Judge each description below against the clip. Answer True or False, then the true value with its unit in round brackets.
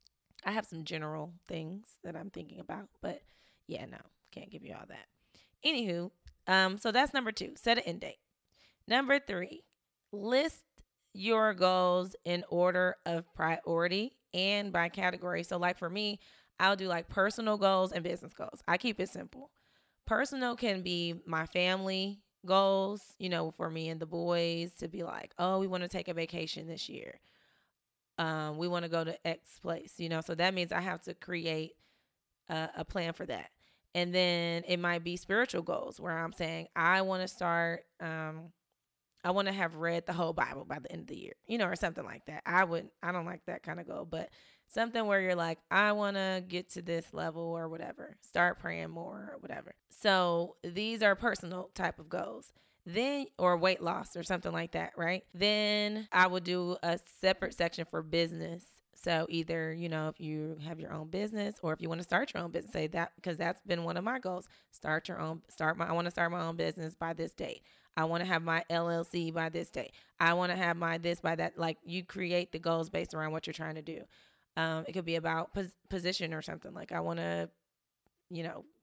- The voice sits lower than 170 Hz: False (175 Hz)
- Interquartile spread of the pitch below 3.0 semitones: True (2.4 semitones)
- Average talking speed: False (210 wpm)